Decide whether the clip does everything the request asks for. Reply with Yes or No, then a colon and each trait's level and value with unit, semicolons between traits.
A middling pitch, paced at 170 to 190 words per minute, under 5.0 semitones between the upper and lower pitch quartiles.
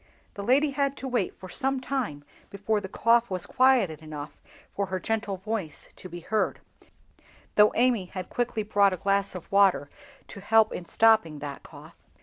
No: high, 200 Hz; average, 175 wpm; average, 4.1 semitones